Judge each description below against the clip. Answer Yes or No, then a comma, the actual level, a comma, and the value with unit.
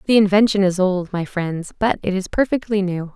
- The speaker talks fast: Yes, fast, 210 wpm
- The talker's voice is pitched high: Yes, high, 195 Hz